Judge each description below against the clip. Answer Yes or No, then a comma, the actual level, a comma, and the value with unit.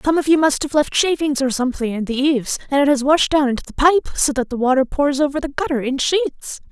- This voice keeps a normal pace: No, fast, 270 wpm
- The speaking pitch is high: Yes, very high, 280 Hz